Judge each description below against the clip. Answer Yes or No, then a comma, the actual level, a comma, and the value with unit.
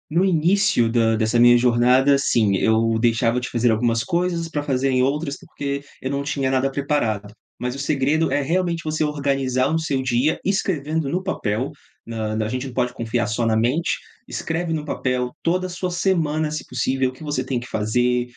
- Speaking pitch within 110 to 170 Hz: Yes, low, 135 Hz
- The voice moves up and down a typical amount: Yes, average, 4.3 semitones